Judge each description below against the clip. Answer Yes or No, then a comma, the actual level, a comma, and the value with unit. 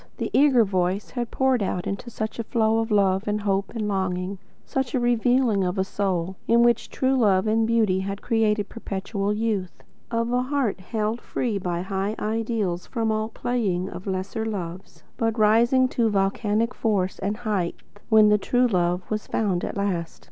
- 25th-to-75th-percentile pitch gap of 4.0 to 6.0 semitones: No, average, 3.3 semitones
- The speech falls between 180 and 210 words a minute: Yes, average, 185 wpm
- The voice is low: No, high, 210 Hz